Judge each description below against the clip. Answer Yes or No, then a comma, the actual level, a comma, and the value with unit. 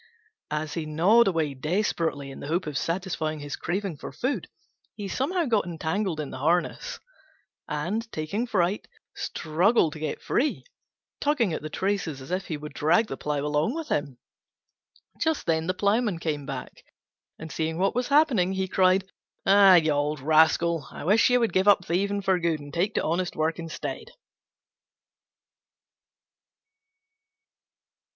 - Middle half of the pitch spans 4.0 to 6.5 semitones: Yes, average, 4.7 semitones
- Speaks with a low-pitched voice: No, medium, 170 Hz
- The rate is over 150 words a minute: Yes, average, 160 wpm